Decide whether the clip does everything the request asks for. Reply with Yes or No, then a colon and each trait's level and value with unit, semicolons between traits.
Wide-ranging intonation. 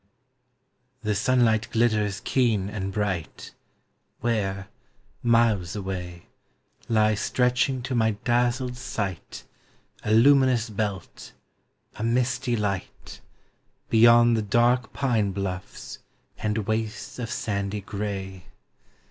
No: average, 3.2 semitones